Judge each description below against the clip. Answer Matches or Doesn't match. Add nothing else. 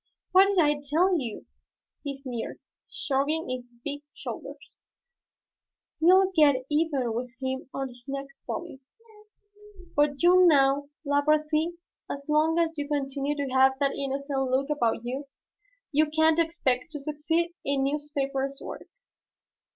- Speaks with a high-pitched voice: Matches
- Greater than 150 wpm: Doesn't match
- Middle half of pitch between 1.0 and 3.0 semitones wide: Matches